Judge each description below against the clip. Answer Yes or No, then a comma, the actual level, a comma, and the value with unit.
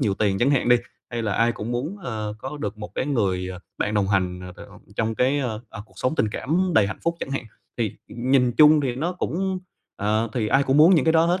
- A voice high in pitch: No, low, 120 Hz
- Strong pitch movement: Yes, wide, 5.7 semitones